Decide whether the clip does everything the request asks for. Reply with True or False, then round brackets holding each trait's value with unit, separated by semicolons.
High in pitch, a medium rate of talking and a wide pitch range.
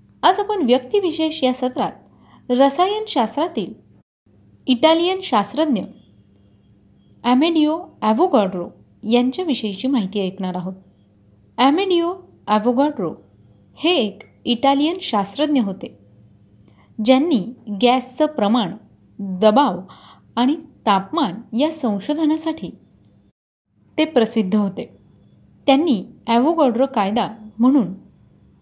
False (245 Hz; 75 wpm; 6.6 semitones)